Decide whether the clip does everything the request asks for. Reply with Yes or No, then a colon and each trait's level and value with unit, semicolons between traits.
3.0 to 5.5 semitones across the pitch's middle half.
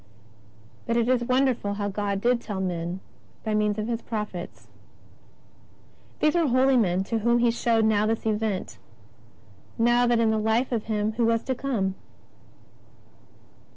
No: narrow, 2.4 semitones